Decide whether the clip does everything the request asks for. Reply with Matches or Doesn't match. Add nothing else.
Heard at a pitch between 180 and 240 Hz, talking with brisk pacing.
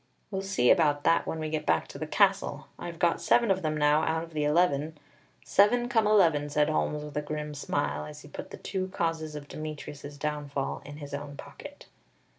Doesn't match